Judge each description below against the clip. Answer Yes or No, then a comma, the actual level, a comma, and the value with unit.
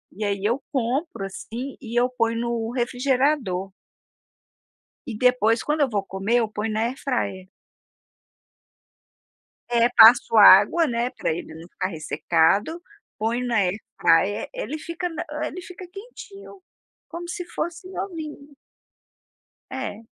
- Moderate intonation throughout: No, wide, 6.2 semitones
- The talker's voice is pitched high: Yes, high, 240 Hz